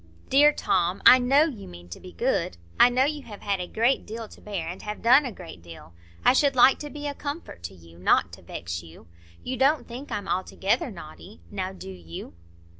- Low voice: No, high, 210 Hz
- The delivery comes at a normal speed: No, fast, 220 wpm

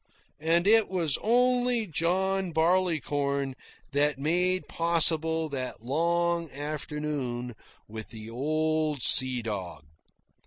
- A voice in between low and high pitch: Yes, medium, 155 Hz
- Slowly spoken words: Yes, slow, 95 wpm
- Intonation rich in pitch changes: No, average, 4.1 semitones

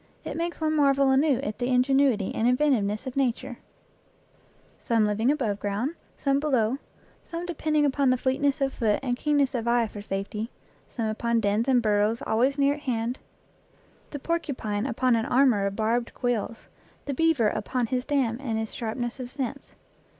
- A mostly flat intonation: No, average, 3.8 semitones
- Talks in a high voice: Yes, very high, 250 Hz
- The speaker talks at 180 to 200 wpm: No, average, 170 wpm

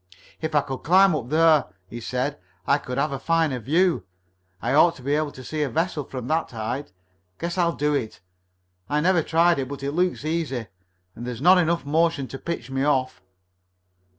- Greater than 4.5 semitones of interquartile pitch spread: No, average, 3.9 semitones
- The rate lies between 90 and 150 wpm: No, average, 200 wpm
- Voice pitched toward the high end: No, medium, 150 Hz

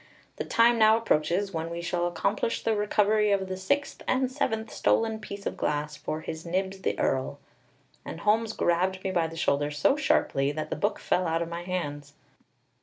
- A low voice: No, medium, 185 Hz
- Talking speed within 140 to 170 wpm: No, average, 190 wpm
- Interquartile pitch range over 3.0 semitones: Yes, average, 4.8 semitones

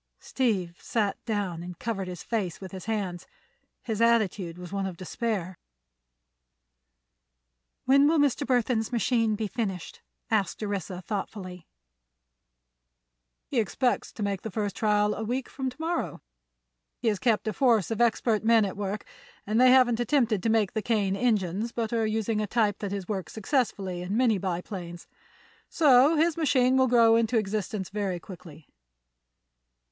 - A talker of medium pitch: No, high, 215 Hz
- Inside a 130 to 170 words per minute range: Yes, average, 155 wpm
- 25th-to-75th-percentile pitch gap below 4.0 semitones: Yes, average, 3.6 semitones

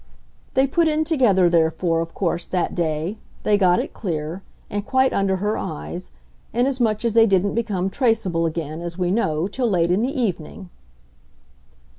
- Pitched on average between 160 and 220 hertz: Yes, high, 190 Hz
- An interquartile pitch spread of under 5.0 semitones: No, wide, 5.4 semitones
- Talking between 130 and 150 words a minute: No, average, 165 wpm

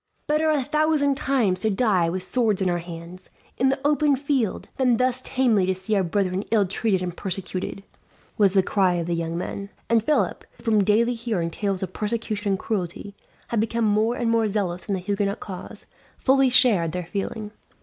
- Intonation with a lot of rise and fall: No, average, 4.5 semitones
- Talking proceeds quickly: No, average, 195 wpm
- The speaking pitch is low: No, high, 205 Hz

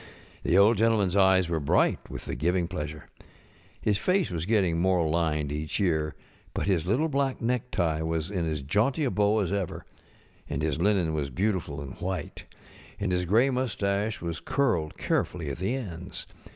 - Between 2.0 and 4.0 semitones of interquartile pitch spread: No, average, 4.8 semitones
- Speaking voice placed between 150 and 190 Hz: No, very low, 90 Hz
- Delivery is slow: No, average, 175 wpm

